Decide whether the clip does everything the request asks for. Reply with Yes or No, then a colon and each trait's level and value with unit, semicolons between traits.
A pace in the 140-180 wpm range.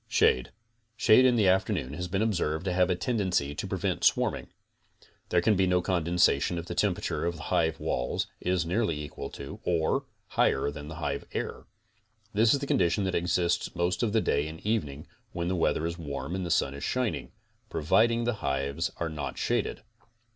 No: average, 200 wpm